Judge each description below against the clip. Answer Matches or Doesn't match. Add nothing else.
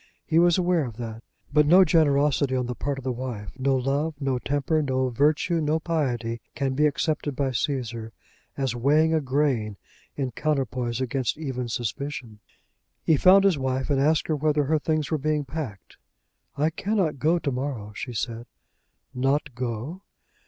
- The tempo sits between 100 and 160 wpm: Doesn't match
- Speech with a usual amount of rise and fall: Matches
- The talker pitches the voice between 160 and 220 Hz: Doesn't match